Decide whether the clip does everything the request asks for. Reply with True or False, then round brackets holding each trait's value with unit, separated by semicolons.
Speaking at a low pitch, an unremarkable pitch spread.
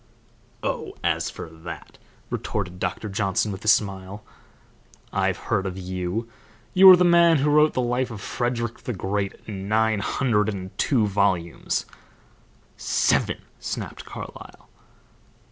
True (105 Hz; 4.2 semitones)